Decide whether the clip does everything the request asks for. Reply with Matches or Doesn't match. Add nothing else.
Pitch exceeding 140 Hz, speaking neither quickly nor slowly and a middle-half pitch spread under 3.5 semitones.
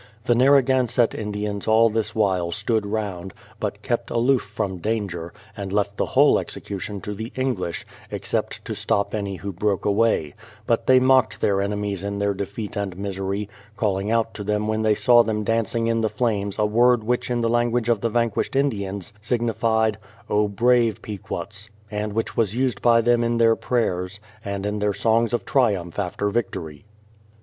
Doesn't match